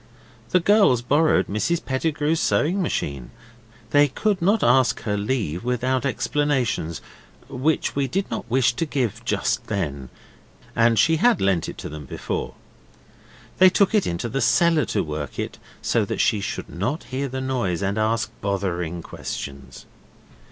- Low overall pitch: Yes, low, 125 Hz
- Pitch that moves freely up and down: Yes, wide, 7.0 semitones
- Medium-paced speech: Yes, average, 155 wpm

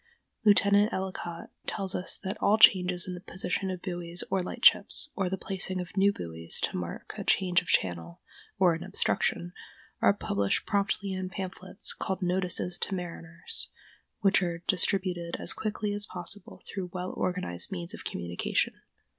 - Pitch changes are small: Yes, narrow, 2.1 semitones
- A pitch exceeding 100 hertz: Yes, medium, 185 Hz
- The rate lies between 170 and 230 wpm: No, average, 160 wpm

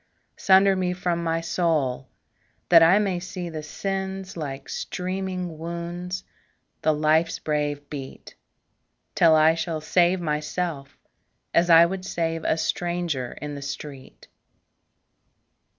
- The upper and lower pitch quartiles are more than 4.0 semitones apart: No, average, 2.8 semitones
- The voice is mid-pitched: Yes, medium, 165 Hz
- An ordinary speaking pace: No, slow, 120 wpm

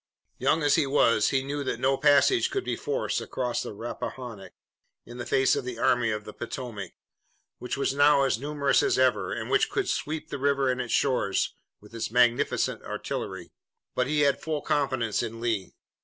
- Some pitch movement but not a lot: Yes, average, 3.6 semitones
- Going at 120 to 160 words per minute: No, average, 190 wpm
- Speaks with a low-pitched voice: Yes, low, 130 Hz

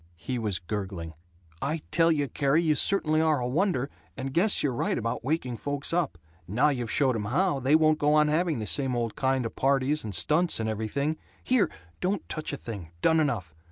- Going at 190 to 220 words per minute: Yes, fast, 205 wpm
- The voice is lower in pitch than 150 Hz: Yes, medium, 140 Hz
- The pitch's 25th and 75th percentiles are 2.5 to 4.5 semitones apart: No, average, 5.2 semitones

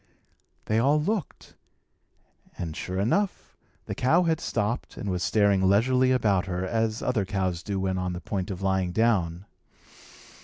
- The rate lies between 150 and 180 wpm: Yes, average, 155 wpm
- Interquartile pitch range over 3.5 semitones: Yes, average, 4.4 semitones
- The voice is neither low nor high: No, low, 100 Hz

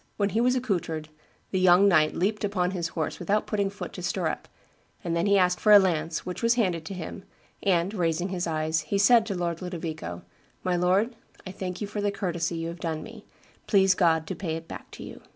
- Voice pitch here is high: No, medium, 180 Hz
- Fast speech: Yes, fast, 220 wpm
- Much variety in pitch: No, average, 3.2 semitones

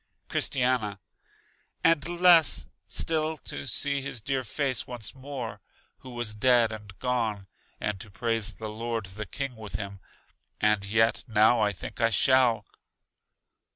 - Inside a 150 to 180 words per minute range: No, average, 140 wpm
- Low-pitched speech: Yes, low, 115 Hz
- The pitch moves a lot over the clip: No, average, 3.7 semitones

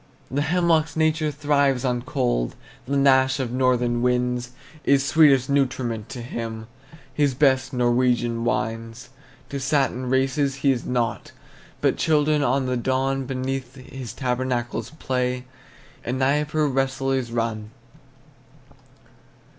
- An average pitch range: No, narrow, 2.3 semitones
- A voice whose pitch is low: Yes, low, 130 Hz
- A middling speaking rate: No, slow, 120 wpm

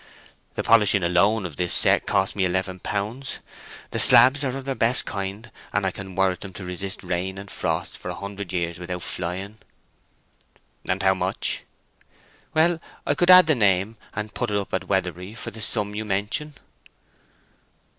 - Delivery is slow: No, average, 175 wpm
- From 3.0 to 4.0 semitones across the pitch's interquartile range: Yes, average, 3.4 semitones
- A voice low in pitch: Yes, low, 100 Hz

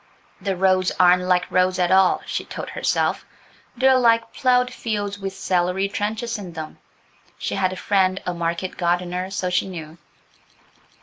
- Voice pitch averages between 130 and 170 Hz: No, medium, 185 Hz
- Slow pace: No, average, 150 wpm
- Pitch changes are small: Yes, narrow, 2.2 semitones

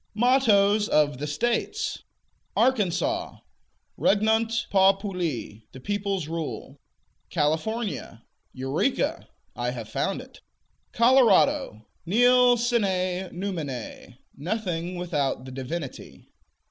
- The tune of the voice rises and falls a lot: Yes, wide, 7.2 semitones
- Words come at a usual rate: No, slow, 85 wpm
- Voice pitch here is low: No, high, 190 Hz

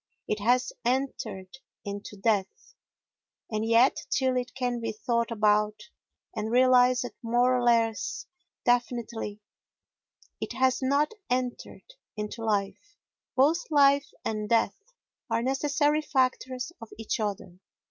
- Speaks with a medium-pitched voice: No, high, 240 Hz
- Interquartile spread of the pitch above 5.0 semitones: No, average, 3.3 semitones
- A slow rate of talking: Yes, slow, 115 wpm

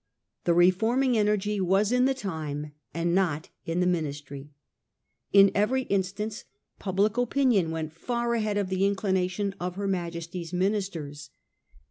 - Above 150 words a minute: No, average, 145 wpm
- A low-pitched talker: No, high, 190 Hz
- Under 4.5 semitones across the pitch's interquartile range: Yes, average, 3.8 semitones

